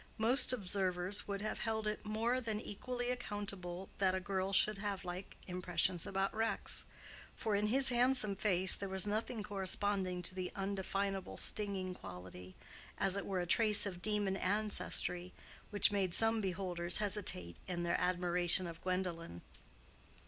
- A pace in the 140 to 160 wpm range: Yes, average, 145 wpm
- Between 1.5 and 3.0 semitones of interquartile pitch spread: Yes, average, 2.7 semitones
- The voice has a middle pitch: No, high, 195 Hz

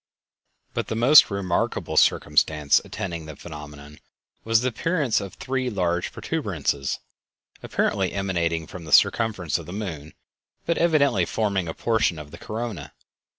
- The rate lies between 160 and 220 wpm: No, average, 140 wpm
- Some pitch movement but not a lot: No, wide, 6.2 semitones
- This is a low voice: Yes, very low, 95 Hz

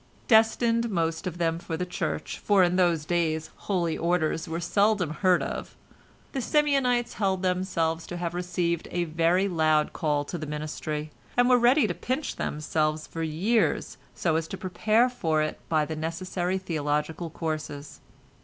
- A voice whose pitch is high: No, medium, 170 Hz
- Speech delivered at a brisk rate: No, average, 165 wpm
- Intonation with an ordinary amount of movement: Yes, average, 3.3 semitones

